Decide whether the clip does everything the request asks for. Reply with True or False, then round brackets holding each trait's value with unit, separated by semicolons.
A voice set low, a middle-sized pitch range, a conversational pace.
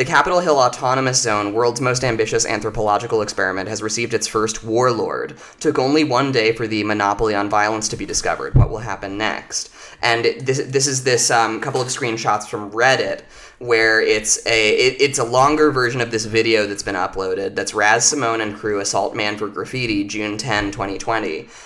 True (115 Hz; 3.4 semitones; 190 wpm)